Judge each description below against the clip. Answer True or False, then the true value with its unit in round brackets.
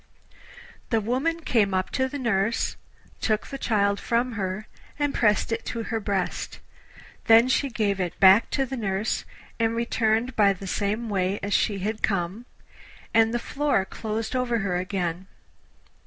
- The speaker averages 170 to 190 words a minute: False (160 wpm)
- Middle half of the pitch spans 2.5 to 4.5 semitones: True (3.3 semitones)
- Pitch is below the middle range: False (220 Hz)